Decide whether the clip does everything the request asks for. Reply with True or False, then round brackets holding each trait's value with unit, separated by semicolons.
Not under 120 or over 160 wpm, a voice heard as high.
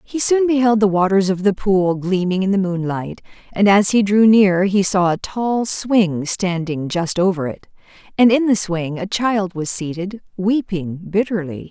False (185 wpm; 195 Hz)